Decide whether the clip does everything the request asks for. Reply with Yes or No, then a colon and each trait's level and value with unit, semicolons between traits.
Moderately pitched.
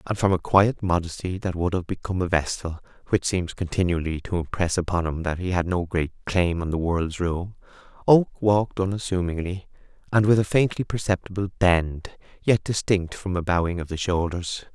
No: very low, 90 Hz